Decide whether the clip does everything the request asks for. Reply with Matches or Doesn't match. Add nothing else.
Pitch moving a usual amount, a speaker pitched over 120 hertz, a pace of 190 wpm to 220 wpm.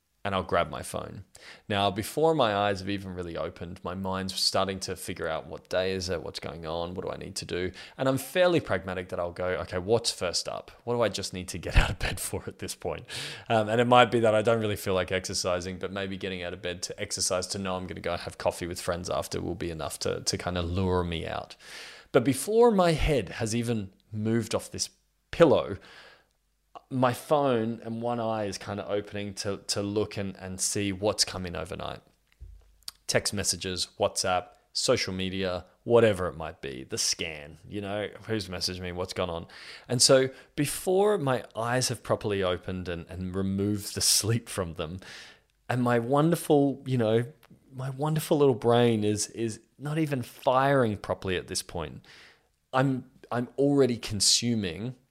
Doesn't match